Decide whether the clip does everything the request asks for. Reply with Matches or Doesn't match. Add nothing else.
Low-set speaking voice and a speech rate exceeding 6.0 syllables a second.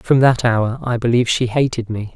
Doesn't match